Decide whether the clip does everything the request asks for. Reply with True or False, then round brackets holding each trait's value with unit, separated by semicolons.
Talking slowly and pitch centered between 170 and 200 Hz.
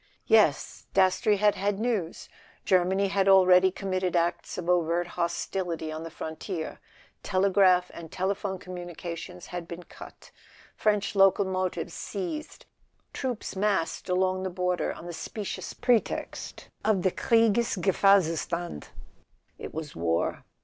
True (130 wpm; 185 Hz)